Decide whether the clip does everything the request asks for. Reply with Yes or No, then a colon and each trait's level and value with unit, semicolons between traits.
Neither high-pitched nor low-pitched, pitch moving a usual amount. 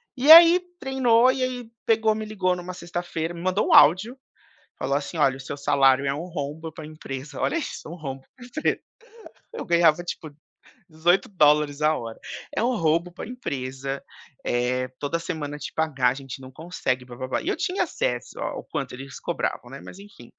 No: medium, 160 Hz; wide, 7.0 semitones